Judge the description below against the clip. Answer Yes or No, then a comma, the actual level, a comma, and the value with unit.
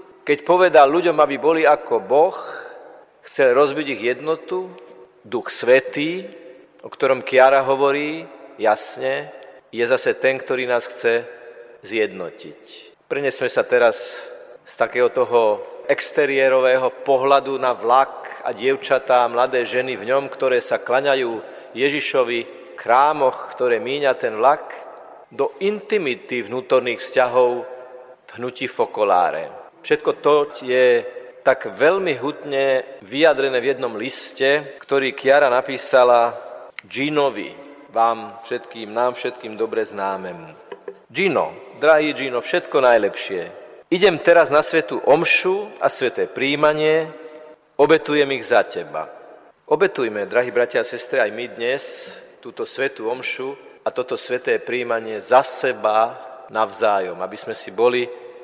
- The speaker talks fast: No, average, 120 wpm